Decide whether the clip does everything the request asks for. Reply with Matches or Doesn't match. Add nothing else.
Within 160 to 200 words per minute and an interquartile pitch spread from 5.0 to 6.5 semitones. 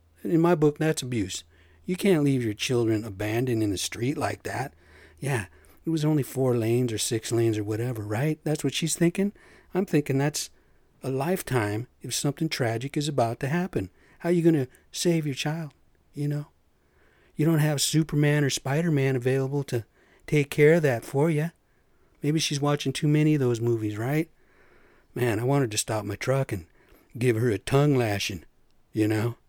Matches